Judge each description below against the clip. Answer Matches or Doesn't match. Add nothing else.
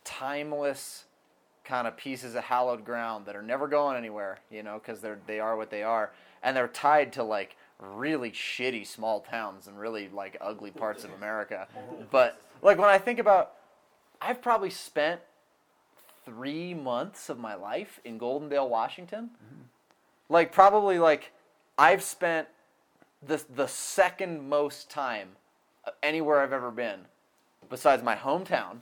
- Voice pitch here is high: Doesn't match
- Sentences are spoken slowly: Doesn't match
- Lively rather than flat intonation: Matches